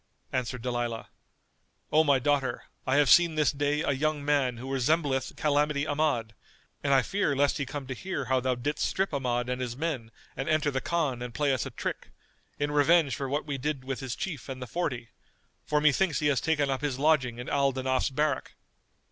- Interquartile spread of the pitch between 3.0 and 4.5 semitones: No, narrow, 2.6 semitones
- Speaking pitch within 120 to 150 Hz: Yes, medium, 140 Hz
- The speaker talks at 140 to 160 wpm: No, fast, 205 wpm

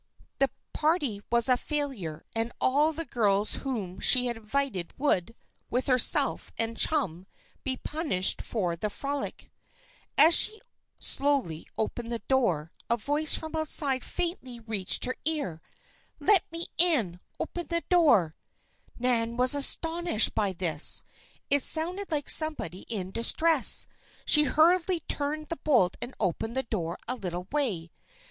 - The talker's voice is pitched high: Yes, very high, 255 Hz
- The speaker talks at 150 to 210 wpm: No, average, 140 wpm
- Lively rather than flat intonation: Yes, wide, 6.9 semitones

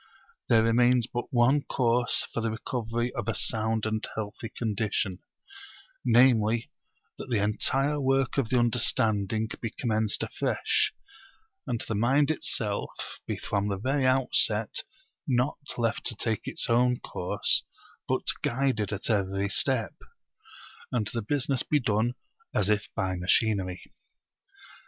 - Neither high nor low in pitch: No, low, 115 Hz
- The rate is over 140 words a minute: No, slow, 135 wpm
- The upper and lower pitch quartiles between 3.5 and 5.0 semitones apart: No, average, 2.7 semitones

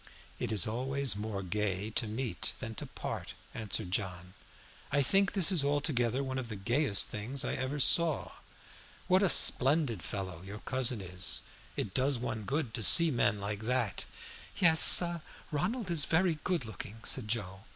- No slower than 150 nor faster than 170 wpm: Yes, average, 165 wpm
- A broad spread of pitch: Yes, wide, 5.7 semitones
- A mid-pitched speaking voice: No, low, 120 Hz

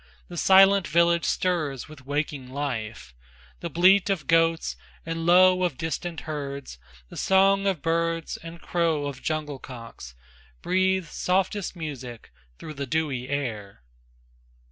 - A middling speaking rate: No, slow, 130 wpm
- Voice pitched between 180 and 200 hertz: No, medium, 160 Hz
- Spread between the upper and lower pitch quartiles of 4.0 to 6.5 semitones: Yes, average, 4.3 semitones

